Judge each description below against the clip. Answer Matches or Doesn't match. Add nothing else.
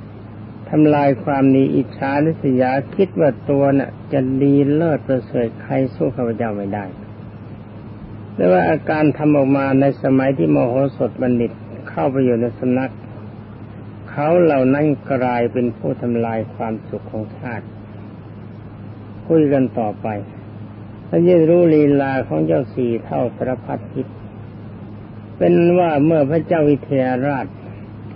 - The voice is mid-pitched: Doesn't match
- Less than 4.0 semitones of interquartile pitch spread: Doesn't match